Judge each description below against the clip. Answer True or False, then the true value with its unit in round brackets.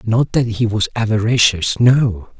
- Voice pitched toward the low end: True (110 Hz)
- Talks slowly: True (125 wpm)